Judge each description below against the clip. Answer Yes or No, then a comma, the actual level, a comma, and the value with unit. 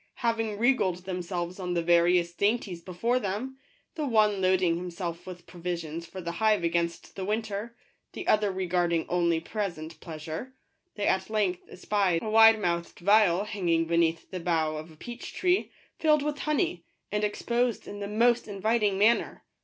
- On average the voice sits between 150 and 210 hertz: Yes, high, 190 Hz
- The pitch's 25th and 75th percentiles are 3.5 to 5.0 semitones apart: Yes, average, 4.3 semitones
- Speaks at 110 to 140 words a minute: No, average, 170 wpm